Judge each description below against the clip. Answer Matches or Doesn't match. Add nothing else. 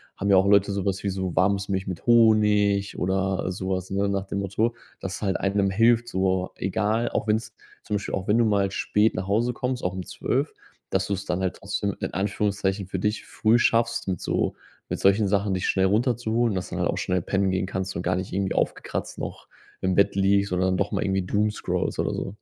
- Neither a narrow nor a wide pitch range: Doesn't match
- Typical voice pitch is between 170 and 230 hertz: Doesn't match